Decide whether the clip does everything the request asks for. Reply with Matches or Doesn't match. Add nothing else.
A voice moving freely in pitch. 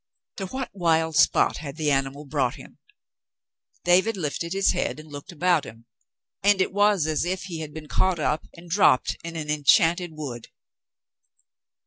Doesn't match